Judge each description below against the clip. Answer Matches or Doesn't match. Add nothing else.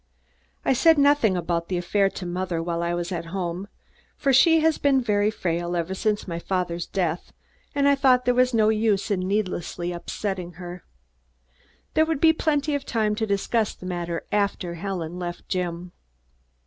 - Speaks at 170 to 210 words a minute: Matches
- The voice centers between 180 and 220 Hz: Matches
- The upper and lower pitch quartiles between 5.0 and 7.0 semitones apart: Matches